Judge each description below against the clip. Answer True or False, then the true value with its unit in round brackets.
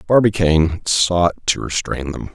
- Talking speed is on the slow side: True (130 wpm)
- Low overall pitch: True (90 Hz)